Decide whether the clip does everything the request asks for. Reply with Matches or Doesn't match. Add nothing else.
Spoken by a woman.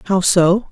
Doesn't match